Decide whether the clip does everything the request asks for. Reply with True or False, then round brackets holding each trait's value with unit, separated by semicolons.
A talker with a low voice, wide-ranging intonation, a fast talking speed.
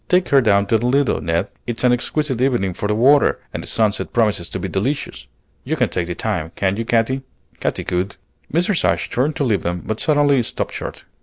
True (115 Hz; 5.8 semitones; 220 wpm)